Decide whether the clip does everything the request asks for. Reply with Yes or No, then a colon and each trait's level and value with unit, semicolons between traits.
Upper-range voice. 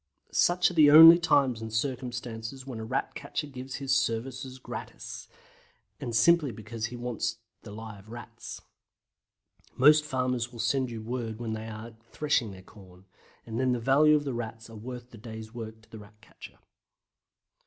No: low, 120 Hz